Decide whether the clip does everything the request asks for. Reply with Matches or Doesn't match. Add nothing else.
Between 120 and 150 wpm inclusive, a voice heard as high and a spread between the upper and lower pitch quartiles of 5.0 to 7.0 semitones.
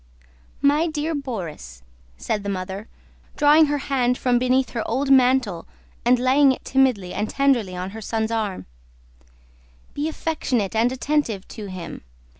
Matches